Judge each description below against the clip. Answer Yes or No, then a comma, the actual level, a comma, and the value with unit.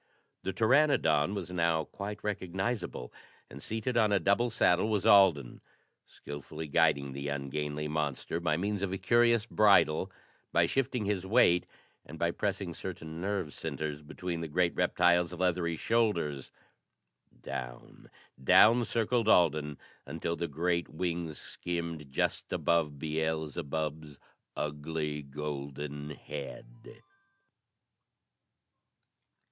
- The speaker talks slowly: Yes, slow, 115 wpm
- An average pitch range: Yes, average, 4.9 semitones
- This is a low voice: Yes, very low, 85 Hz